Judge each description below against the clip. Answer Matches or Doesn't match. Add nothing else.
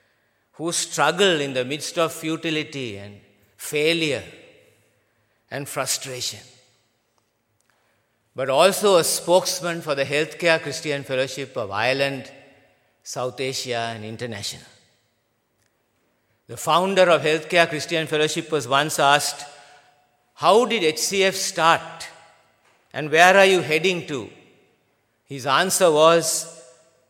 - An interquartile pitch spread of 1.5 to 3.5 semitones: Doesn't match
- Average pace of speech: Doesn't match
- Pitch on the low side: Doesn't match